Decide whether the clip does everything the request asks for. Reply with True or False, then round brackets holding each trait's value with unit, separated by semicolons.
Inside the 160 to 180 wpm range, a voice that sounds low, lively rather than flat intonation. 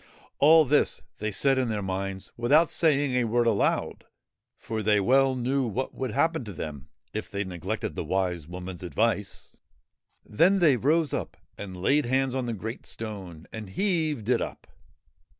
True (170 wpm; 115 Hz; 5.7 semitones)